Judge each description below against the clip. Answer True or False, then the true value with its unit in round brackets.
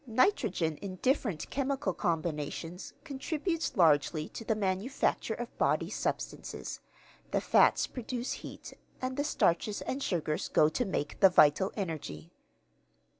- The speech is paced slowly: True (125 wpm)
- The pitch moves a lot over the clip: True (7.9 semitones)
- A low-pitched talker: False (195 Hz)